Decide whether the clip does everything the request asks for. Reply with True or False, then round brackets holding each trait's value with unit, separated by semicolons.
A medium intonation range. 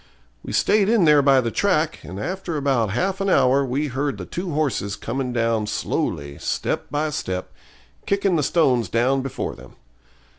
False (6.1 semitones)